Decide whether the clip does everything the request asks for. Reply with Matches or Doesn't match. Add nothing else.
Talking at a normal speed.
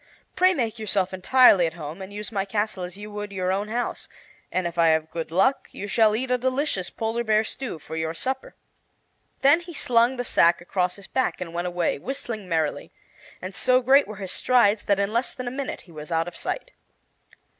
Doesn't match